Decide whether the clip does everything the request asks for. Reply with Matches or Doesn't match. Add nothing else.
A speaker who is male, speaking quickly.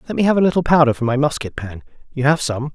Matches